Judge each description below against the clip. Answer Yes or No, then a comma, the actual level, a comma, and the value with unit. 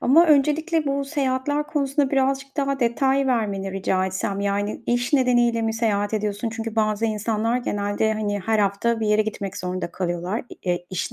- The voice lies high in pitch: Yes, high, 225 Hz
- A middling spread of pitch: Yes, average, 4.8 semitones